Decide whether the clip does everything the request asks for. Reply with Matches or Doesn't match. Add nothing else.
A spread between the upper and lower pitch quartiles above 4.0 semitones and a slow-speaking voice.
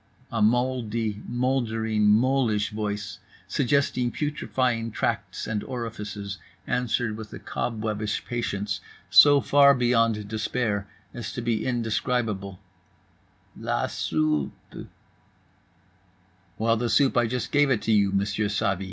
Doesn't match